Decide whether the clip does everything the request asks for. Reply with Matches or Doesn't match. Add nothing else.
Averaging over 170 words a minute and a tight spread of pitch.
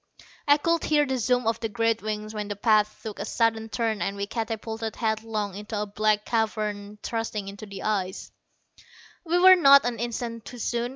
Matches